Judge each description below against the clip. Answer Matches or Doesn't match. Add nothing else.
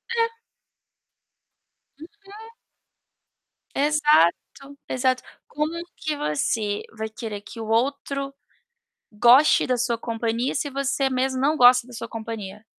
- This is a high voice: Matches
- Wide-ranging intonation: Doesn't match